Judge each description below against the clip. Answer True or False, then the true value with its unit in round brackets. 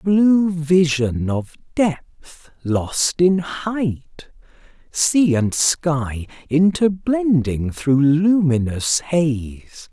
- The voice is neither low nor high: True (155 Hz)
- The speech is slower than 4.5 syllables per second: True (2.4 syllables/s)